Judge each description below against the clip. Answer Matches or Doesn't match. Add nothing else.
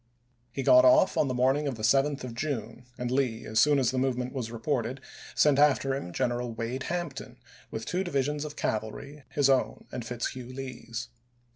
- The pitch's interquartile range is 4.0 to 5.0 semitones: Doesn't match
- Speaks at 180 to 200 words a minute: Matches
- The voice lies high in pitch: Doesn't match